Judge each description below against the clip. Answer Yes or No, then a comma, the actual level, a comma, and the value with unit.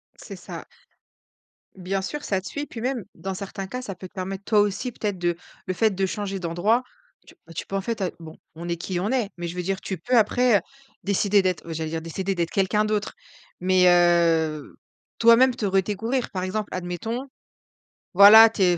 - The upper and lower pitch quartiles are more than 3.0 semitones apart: Yes, average, 3.4 semitones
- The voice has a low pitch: No, high, 195 Hz